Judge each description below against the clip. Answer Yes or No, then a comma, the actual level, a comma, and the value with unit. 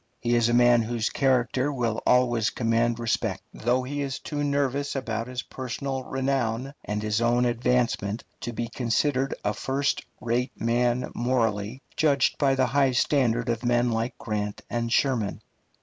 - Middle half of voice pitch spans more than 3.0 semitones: No, narrow, 2.4 semitones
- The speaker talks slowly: No, average, 160 wpm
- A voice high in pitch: No, low, 120 Hz